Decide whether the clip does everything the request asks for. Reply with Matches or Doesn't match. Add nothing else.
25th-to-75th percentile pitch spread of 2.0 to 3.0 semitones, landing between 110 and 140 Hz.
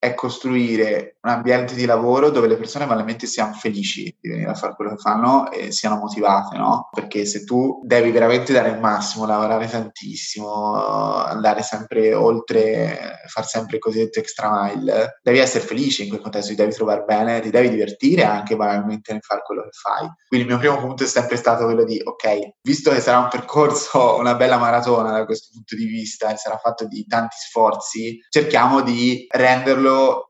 Matches